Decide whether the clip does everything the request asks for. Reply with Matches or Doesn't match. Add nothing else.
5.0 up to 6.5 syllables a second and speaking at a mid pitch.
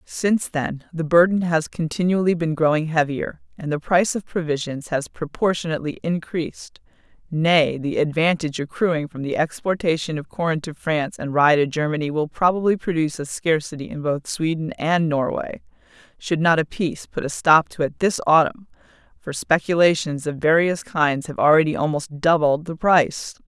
Matches